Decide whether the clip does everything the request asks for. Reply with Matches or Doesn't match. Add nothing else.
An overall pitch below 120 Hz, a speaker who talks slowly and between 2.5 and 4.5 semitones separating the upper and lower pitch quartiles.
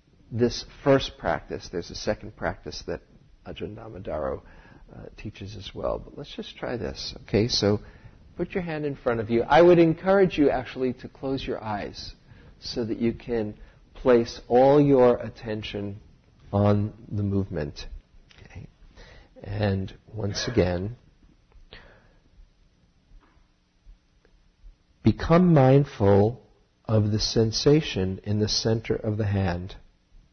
Matches